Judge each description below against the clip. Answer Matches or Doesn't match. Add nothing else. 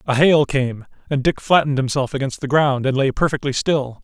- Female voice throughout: Doesn't match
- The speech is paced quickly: Matches